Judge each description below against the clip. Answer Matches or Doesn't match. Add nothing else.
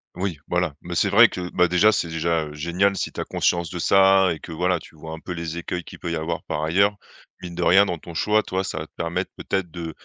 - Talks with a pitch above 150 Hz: Doesn't match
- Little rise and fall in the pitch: Matches